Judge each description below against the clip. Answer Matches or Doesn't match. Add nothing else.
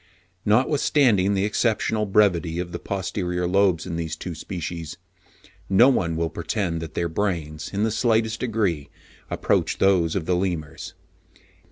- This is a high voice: Doesn't match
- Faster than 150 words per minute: Doesn't match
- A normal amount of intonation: Matches